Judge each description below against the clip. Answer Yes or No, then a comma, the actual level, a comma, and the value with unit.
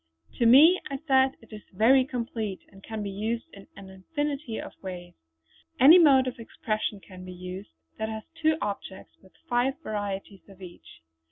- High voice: Yes, high, 220 Hz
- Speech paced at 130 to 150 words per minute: No, average, 175 wpm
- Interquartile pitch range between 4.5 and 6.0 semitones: Yes, average, 5.3 semitones